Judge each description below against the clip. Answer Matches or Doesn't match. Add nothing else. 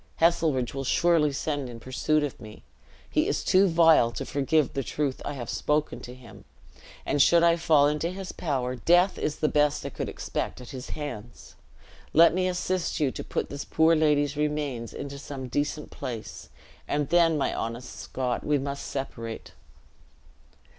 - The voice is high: Doesn't match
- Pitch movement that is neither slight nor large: Matches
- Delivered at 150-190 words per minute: Matches